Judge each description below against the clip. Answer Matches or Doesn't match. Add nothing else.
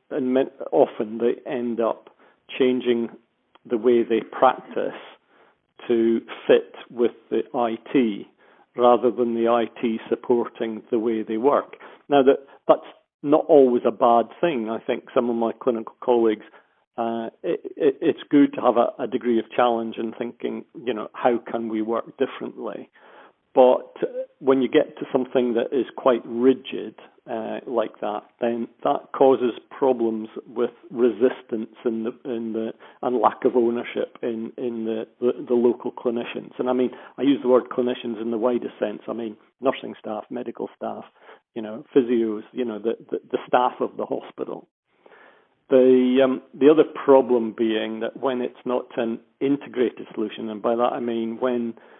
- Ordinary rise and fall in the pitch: Doesn't match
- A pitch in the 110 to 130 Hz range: Matches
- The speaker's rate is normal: Matches